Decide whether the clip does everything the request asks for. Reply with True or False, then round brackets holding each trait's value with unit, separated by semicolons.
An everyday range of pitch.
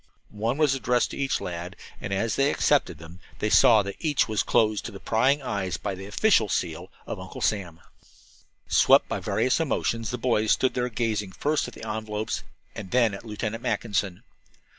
True (3.9 semitones)